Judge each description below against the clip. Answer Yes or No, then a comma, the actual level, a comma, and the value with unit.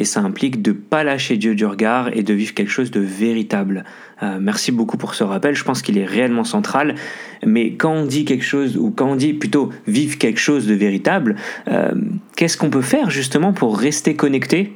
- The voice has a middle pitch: Yes, medium, 145 Hz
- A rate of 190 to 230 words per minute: Yes, fast, 220 wpm